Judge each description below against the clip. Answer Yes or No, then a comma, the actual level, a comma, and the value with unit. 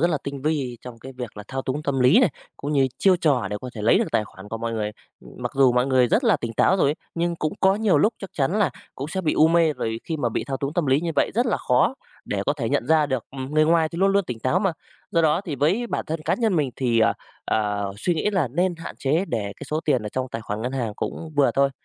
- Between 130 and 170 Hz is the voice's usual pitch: Yes, medium, 140 Hz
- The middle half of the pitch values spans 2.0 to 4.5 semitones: No, average, 5.2 semitones